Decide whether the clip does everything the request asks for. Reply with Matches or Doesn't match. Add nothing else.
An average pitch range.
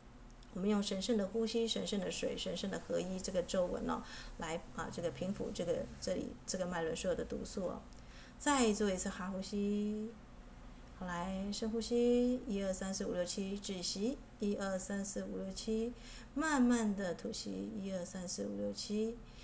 Matches